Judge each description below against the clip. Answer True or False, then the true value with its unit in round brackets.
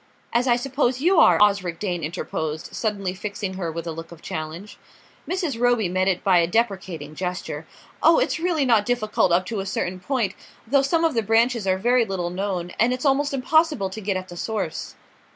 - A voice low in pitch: False (205 Hz)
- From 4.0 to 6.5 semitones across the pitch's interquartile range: True (5.3 semitones)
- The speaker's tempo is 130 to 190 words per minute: False (205 wpm)